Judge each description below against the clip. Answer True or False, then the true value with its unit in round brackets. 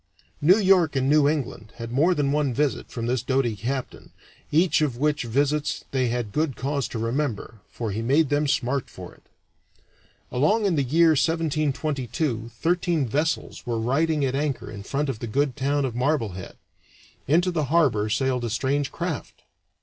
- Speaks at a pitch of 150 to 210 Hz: False (140 Hz)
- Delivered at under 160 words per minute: False (175 wpm)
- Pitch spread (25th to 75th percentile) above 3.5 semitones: True (4.0 semitones)